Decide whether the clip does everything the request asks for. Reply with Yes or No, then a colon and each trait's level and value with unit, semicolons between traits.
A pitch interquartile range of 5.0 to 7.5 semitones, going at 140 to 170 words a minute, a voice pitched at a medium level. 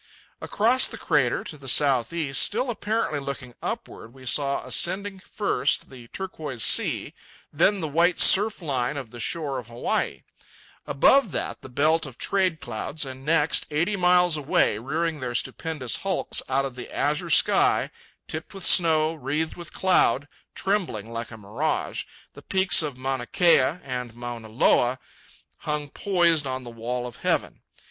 Yes: wide, 5.4 semitones; average, 160 wpm; medium, 145 Hz